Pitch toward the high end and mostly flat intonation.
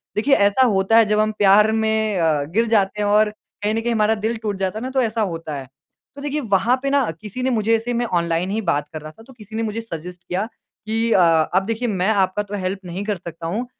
No: high, 210 Hz; average, 3.4 semitones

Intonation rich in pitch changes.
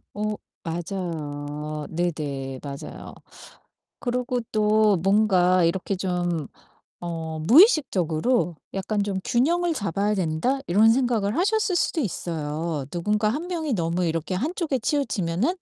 Yes: wide, 6.6 semitones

